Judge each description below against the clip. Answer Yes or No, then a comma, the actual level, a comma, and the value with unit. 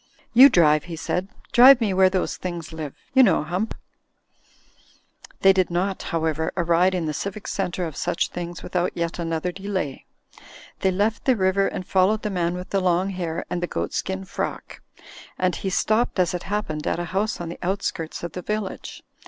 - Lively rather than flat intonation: No, narrow, 2.5 semitones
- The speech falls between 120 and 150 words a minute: No, average, 185 wpm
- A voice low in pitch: No, medium, 185 Hz